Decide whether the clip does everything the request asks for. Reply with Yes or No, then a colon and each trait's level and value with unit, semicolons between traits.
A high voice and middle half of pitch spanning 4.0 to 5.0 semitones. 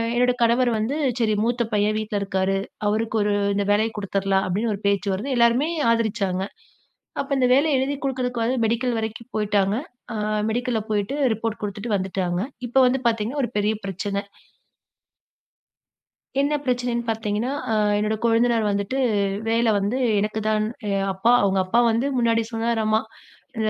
No: high, 220 Hz; average, 2.7 semitones